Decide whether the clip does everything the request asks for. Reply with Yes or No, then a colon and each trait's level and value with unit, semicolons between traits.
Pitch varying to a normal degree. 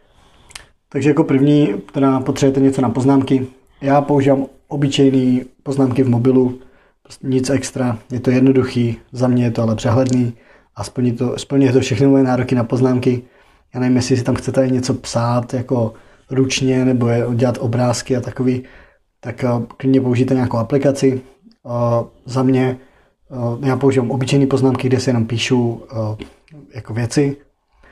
No: narrow, 1.6 semitones